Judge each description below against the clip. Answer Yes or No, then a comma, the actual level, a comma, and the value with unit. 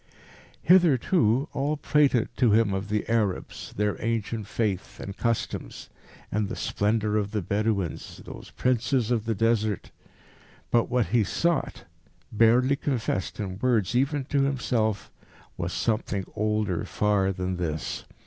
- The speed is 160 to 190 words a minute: No, average, 140 wpm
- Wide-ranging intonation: No, average, 3.4 semitones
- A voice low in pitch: Yes, low, 110 Hz